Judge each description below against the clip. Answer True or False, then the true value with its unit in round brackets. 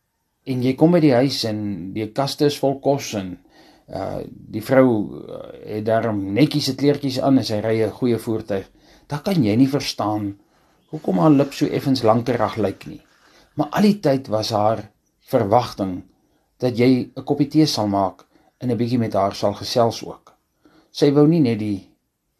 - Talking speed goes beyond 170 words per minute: True (180 wpm)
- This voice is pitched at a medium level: False (125 Hz)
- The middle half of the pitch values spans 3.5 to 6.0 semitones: True (4.9 semitones)